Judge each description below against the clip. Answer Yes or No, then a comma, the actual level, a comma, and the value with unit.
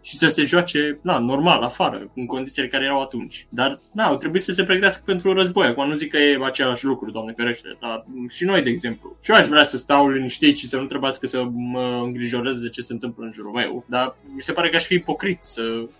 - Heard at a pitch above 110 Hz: Yes, low, 135 Hz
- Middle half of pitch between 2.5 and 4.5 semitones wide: Yes, average, 4.1 semitones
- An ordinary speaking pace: No, fast, 245 wpm